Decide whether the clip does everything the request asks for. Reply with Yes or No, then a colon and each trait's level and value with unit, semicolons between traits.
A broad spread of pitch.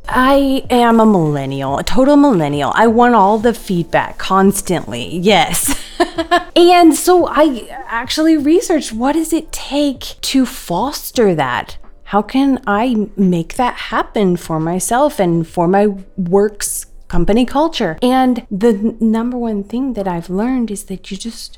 Yes: wide, 5.7 semitones